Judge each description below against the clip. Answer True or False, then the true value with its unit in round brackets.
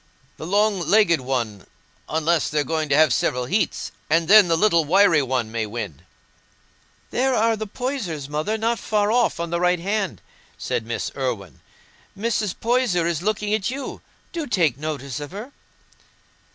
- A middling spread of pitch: False (7.0 semitones)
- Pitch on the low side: False (170 Hz)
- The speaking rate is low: False (165 wpm)